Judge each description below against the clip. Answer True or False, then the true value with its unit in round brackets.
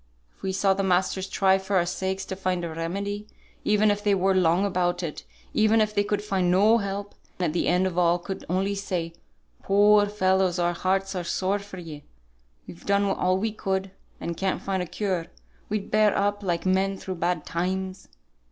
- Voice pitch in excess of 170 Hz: True (190 Hz)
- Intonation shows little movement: True (2.0 semitones)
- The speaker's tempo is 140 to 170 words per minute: False (200 wpm)